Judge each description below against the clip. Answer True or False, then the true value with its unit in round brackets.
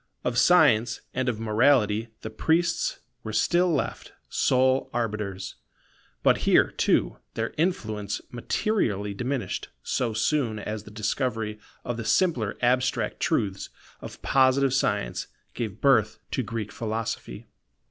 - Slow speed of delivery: True (125 wpm)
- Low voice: True (115 Hz)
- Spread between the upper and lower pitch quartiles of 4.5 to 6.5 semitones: False (3.8 semitones)